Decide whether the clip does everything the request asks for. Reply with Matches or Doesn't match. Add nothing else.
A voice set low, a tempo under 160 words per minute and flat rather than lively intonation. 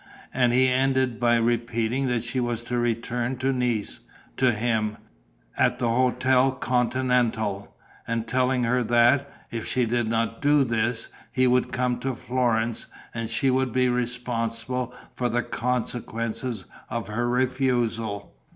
Matches